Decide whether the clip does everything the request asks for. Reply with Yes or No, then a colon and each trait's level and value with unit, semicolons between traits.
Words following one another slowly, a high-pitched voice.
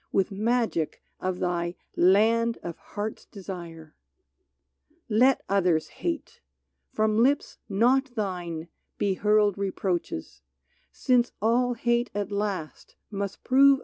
Yes: slow, 120 wpm; high, 205 Hz